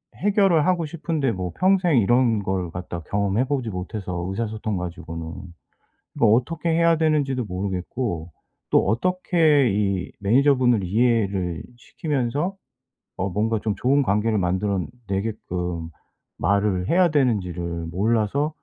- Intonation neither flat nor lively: No, wide, 7.3 semitones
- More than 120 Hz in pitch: No, low, 110 Hz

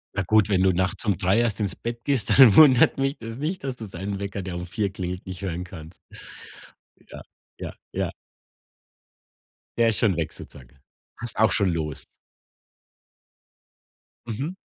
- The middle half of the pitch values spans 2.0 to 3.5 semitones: No, average, 4.3 semitones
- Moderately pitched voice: No, low, 100 Hz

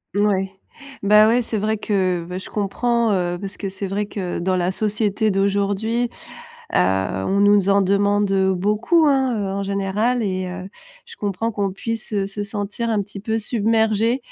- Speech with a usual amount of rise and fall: No, narrow, 2.2 semitones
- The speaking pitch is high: Yes, high, 205 Hz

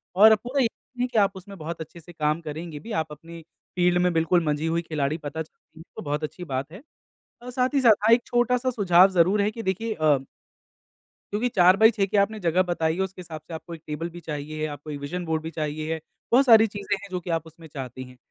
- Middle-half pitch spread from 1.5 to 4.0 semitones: No, average, 4.8 semitones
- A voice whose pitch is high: No, medium, 175 Hz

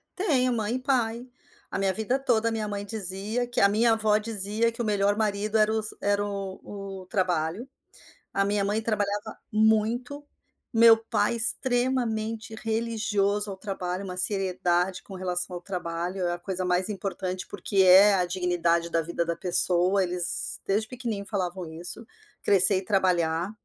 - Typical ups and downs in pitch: Yes, average, 3.3 semitones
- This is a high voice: Yes, high, 200 Hz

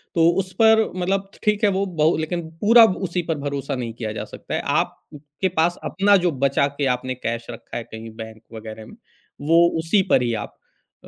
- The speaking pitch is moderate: Yes, medium, 155 Hz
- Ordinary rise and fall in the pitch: No, wide, 7.2 semitones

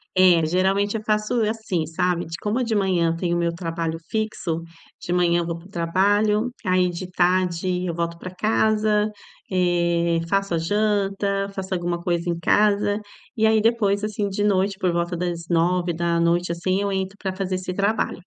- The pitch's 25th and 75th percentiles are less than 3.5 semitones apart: Yes, average, 3.0 semitones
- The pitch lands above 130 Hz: Yes, medium, 185 Hz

